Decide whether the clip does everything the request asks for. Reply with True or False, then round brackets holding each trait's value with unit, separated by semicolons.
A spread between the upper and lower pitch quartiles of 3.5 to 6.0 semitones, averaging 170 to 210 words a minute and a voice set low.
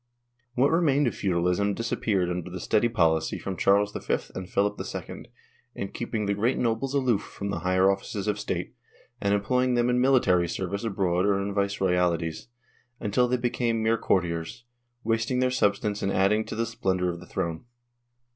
True (4.1 semitones; 175 wpm; 100 Hz)